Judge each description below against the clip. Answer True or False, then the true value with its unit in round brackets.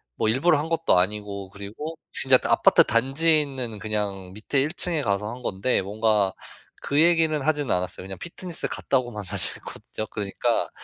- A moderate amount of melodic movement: False (6.7 semitones)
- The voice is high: False (115 Hz)